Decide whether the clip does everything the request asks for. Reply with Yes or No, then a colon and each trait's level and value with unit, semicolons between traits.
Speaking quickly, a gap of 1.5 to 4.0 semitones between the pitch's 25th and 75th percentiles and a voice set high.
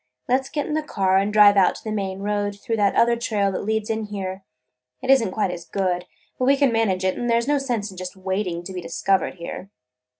Yes: fast, 260 wpm; average, 3.6 semitones; high, 205 Hz